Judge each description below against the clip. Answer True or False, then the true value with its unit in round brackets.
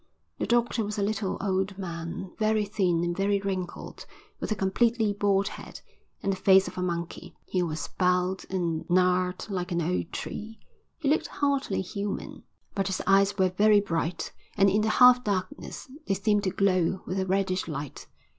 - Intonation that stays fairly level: True (2.1 semitones)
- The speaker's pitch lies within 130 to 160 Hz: False (195 Hz)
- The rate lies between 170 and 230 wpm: True (180 wpm)